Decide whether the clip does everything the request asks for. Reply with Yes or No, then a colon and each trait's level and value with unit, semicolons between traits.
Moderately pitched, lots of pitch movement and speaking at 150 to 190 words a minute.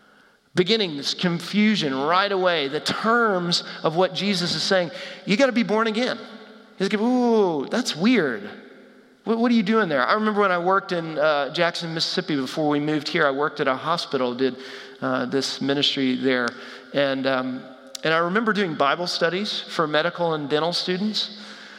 Yes: medium, 175 Hz; wide, 6.3 semitones; average, 180 wpm